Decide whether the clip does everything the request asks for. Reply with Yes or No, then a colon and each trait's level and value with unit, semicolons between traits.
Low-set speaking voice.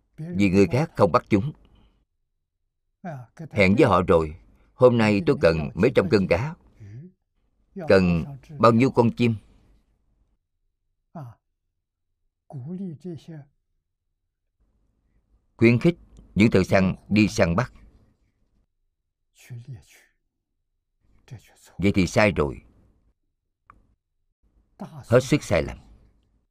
Yes: low, 100 Hz